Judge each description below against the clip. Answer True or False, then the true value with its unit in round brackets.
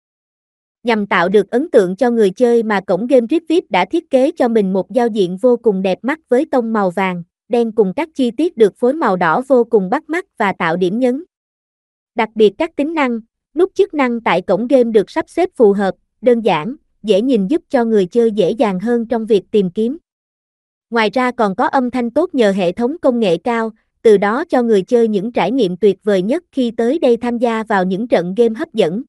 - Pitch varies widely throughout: False (4.0 semitones)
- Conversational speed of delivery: True (230 wpm)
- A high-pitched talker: True (235 Hz)